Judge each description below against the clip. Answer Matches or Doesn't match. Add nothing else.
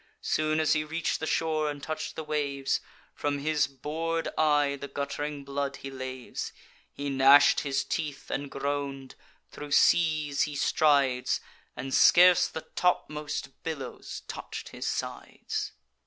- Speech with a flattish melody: Matches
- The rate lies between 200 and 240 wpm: Doesn't match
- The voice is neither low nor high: Matches